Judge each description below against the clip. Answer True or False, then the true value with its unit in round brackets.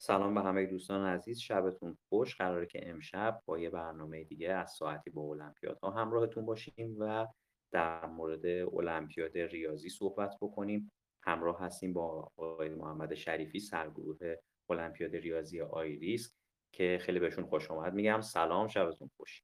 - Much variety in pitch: False (4.1 semitones)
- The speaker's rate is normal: True (145 wpm)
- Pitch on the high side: False (90 Hz)